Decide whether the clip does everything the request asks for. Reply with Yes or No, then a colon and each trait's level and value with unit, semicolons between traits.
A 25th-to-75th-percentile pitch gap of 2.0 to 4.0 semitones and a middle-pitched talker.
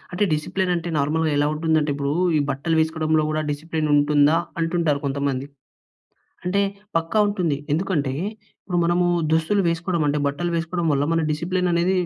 Yes: average, 2.9 semitones; medium, 160 Hz